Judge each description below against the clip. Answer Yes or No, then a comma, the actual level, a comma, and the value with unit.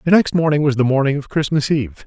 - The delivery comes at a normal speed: No, fast, 260 wpm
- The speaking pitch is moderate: Yes, medium, 145 Hz